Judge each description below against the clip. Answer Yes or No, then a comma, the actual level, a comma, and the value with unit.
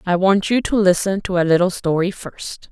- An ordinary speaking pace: No, fast, 220 wpm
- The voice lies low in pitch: No, medium, 185 Hz